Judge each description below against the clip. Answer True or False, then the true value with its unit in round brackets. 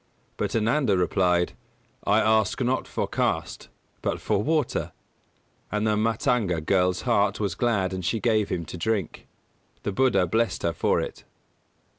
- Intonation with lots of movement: False (3.8 semitones)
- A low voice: True (105 Hz)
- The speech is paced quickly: False (150 wpm)